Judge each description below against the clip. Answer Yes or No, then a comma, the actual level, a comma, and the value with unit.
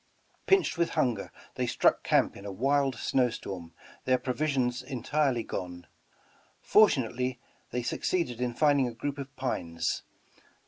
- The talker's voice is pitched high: No, low, 125 Hz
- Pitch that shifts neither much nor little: Yes, average, 3.3 semitones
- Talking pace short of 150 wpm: Yes, slow, 135 wpm